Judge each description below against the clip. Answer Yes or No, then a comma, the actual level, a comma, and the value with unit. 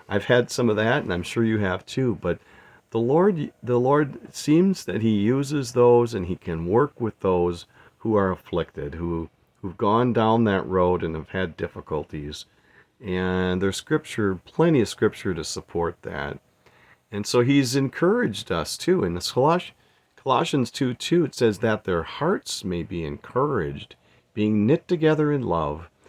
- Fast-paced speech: No, average, 170 wpm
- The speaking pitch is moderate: No, low, 105 Hz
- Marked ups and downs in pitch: Yes, wide, 6.0 semitones